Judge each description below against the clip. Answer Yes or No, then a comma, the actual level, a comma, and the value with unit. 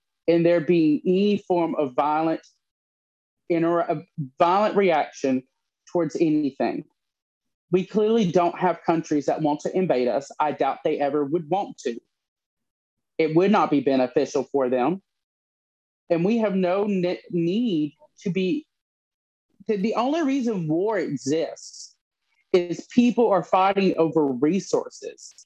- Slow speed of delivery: Yes, slow, 130 wpm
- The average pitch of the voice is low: No, medium, 175 Hz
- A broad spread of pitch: No, average, 4.9 semitones